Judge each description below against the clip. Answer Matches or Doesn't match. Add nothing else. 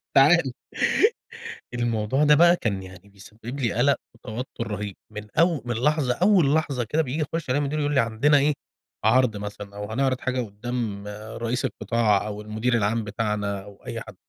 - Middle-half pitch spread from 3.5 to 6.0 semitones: Matches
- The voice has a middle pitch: Doesn't match